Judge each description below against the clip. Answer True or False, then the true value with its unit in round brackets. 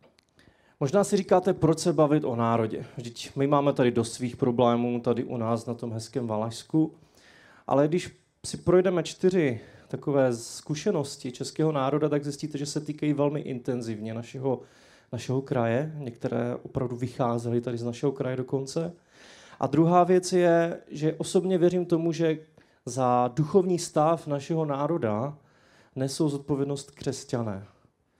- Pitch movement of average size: True (4.5 semitones)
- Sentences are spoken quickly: False (140 wpm)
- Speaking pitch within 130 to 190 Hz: True (140 Hz)